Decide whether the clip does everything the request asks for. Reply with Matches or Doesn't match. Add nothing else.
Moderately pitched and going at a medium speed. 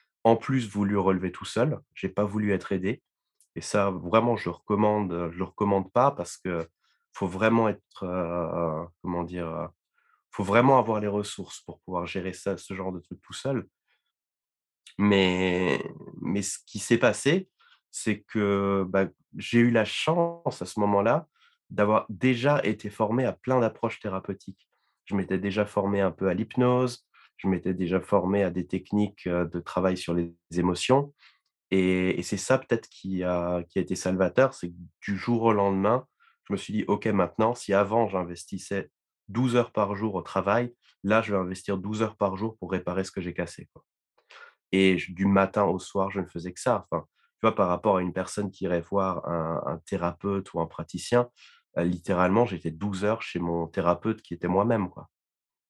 Doesn't match